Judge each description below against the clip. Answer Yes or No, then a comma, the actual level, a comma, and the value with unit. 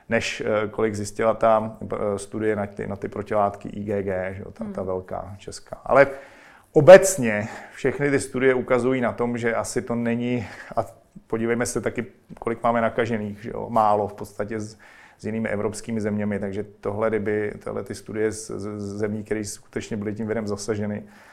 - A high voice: No, low, 110 Hz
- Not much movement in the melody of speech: Yes, narrow, 2.1 semitones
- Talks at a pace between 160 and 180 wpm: Yes, fast, 170 wpm